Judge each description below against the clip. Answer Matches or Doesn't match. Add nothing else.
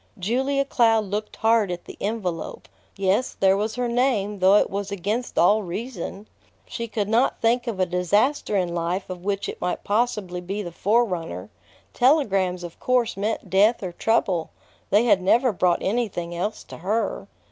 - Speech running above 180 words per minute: Doesn't match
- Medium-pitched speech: Doesn't match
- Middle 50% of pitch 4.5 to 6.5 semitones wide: Doesn't match